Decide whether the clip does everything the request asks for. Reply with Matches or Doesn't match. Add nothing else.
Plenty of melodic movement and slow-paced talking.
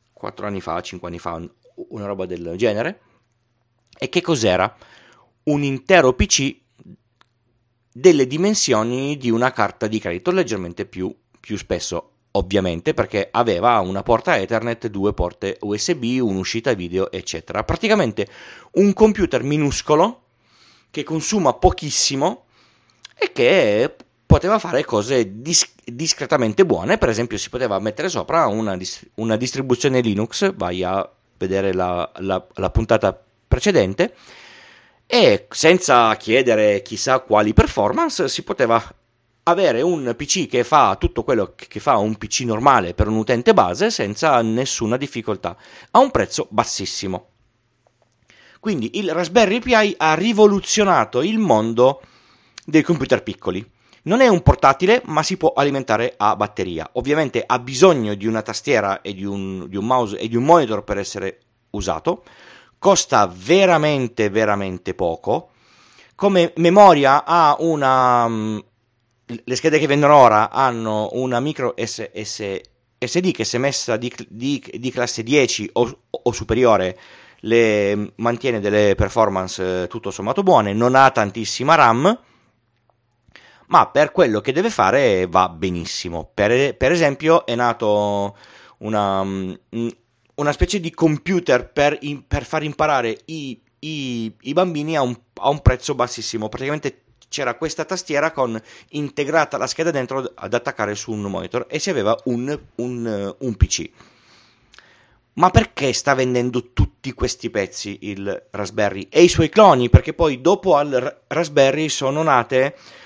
Doesn't match